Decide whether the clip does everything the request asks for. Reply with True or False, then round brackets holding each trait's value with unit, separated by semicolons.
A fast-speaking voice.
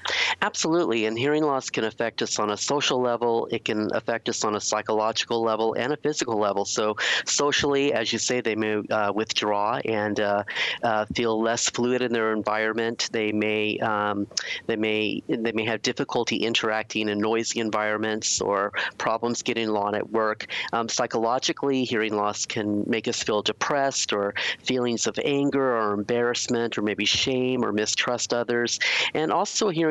False (170 wpm)